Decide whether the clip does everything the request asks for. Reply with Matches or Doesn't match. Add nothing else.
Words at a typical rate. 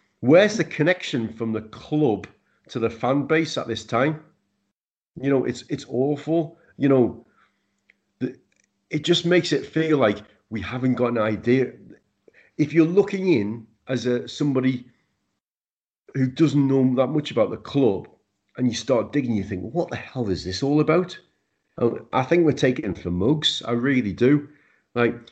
Matches